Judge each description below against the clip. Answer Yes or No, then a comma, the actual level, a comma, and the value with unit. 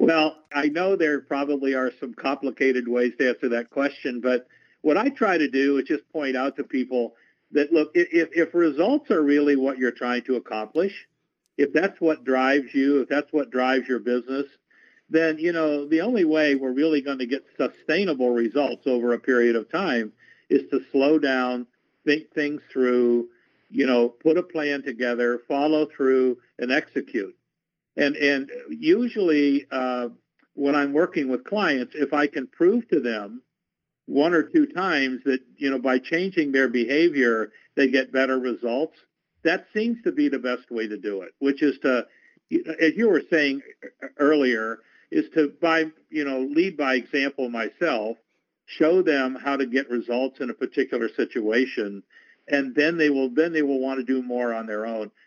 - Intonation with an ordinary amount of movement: Yes, average, 3.5 semitones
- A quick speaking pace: No, average, 180 wpm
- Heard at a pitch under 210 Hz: Yes, medium, 140 Hz